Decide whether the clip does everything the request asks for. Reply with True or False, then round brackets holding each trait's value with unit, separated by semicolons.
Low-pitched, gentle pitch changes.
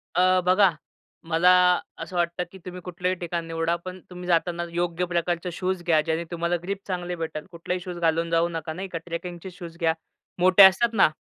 False (175 Hz; 1.4 semitones)